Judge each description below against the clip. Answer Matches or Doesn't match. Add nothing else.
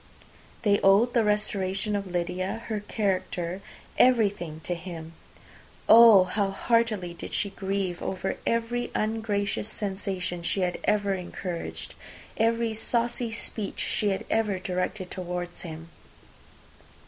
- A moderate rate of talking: Doesn't match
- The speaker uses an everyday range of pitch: Matches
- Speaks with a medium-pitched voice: Doesn't match